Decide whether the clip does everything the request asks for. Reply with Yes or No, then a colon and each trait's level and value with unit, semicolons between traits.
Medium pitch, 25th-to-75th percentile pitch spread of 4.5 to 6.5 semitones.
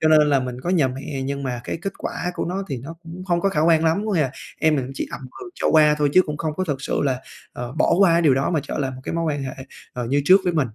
No: medium, 150 Hz; average, 4.1 semitones